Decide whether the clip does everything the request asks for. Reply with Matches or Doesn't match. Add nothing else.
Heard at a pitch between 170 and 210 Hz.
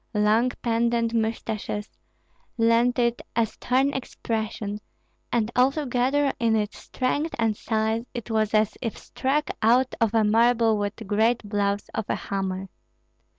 Doesn't match